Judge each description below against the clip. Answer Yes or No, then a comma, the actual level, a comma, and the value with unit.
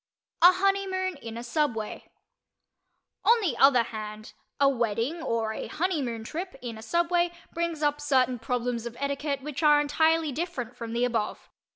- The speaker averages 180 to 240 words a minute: No, average, 160 wpm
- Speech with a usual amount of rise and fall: No, wide, 5.9 semitones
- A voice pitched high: Yes, very high, 280 Hz